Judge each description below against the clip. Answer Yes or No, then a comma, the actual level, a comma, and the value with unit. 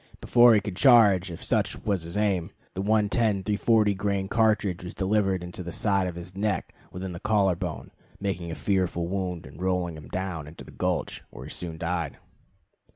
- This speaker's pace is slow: No, average, 190 wpm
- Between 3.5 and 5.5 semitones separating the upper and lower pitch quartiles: No, average, 2.9 semitones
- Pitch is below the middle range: Yes, very low, 95 Hz